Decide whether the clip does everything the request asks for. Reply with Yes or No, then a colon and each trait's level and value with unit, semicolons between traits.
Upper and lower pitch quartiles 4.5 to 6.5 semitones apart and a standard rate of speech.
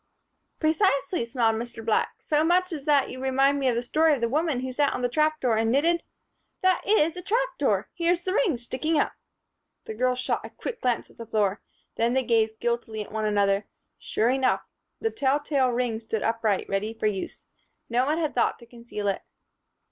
No: average, 5.3 semitones; fast, 215 wpm